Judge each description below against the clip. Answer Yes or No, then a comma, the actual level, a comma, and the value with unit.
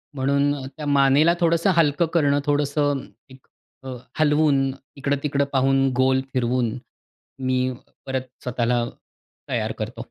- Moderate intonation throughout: No, narrow, 1.9 semitones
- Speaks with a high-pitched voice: No, medium, 140 Hz